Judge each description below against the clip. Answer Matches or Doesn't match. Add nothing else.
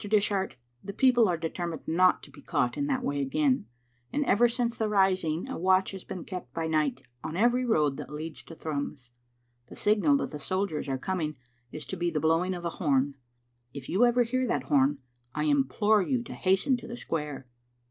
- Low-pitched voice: Doesn't match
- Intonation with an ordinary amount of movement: Doesn't match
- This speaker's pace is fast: Matches